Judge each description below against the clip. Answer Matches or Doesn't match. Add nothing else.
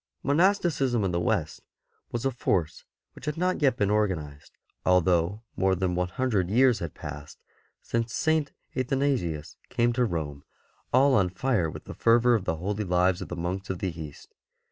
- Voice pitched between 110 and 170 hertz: Doesn't match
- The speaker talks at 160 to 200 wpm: Matches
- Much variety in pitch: Matches